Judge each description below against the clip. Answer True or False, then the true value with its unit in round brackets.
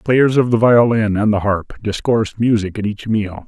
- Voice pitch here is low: True (110 Hz)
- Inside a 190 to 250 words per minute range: True (205 wpm)